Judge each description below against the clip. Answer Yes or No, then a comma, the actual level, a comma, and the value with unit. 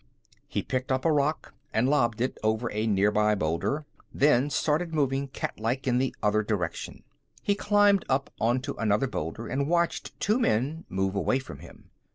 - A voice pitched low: Yes, low, 130 Hz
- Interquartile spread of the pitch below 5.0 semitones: No, wide, 5.5 semitones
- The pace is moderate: Yes, average, 175 wpm